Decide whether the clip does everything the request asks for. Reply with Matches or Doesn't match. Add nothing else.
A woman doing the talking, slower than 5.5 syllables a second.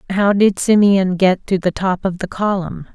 Matches